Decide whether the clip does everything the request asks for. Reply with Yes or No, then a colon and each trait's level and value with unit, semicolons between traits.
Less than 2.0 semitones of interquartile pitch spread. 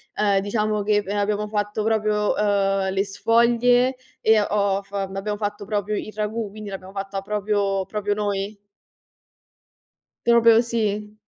Yes: narrow, 1.2 semitones